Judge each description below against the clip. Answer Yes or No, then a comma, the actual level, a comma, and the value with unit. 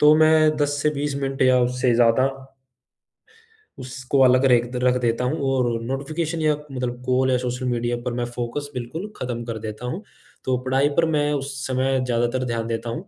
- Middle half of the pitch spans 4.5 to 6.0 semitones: No, average, 2.8 semitones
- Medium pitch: No, low, 130 Hz